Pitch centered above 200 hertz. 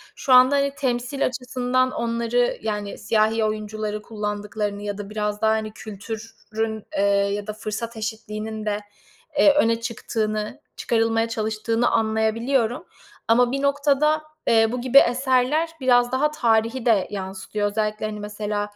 Yes: high, 225 Hz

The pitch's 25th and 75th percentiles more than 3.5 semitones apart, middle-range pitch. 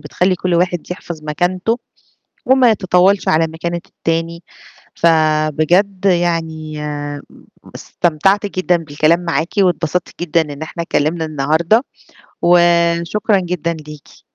No: narrow, 2.4 semitones; medium, 170 Hz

